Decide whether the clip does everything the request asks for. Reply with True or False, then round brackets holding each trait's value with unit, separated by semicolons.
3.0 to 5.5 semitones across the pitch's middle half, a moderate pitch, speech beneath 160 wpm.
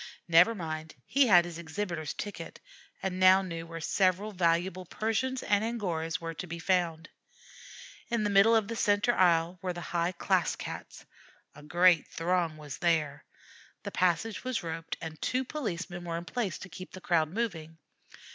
False (3.6 semitones; 175 Hz; 170 wpm)